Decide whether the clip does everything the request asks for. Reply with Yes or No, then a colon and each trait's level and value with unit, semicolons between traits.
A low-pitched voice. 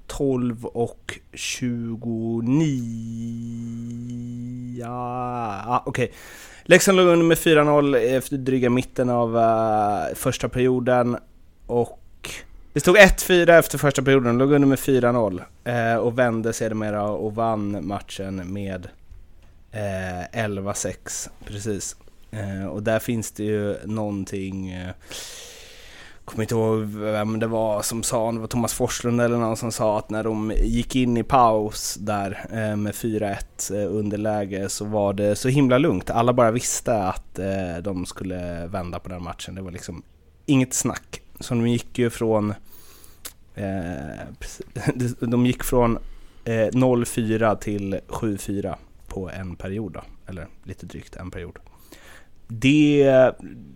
Yes: low, 110 Hz